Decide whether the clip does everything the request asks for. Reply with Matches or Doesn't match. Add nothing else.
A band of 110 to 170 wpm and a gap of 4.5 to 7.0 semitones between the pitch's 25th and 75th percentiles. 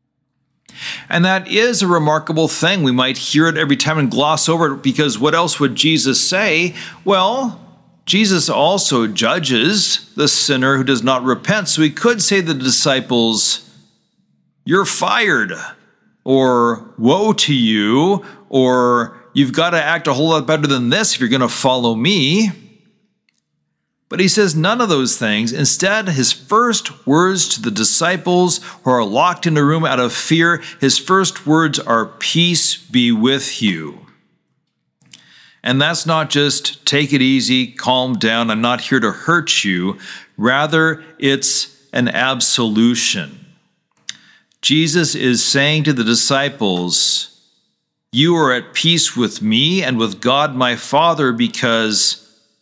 Matches